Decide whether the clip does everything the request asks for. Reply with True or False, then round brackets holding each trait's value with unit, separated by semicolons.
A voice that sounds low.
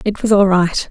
False (195 Hz)